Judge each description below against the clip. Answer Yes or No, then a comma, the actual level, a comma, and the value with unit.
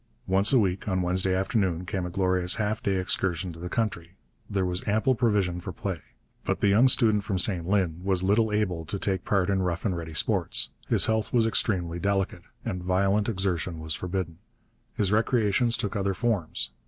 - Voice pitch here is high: No, very low, 95 Hz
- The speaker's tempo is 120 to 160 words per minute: No, average, 190 wpm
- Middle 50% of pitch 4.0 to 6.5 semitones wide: No, narrow, 2.6 semitones